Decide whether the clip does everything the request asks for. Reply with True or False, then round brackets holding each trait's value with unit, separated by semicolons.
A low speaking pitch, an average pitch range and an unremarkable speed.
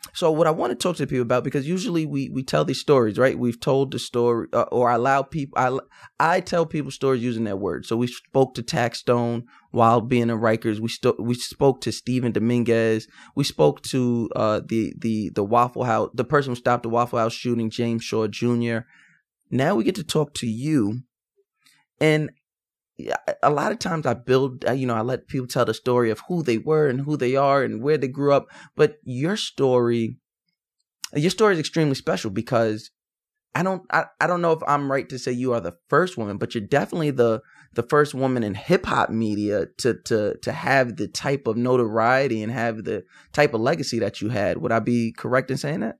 False (125 Hz; 3.8 semitones; 215 wpm)